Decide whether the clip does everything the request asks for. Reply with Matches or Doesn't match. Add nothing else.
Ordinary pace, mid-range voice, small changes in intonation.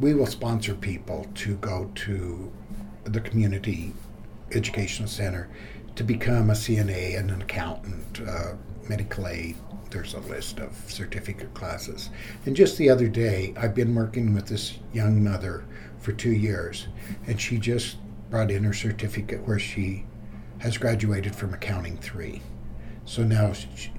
Doesn't match